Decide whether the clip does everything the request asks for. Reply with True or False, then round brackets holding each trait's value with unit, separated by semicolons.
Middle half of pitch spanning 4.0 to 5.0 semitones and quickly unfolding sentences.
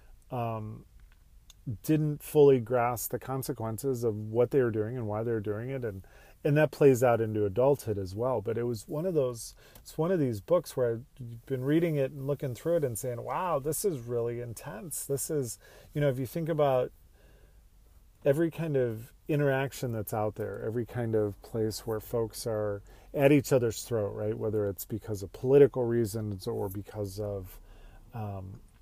False (4.4 semitones; 185 wpm)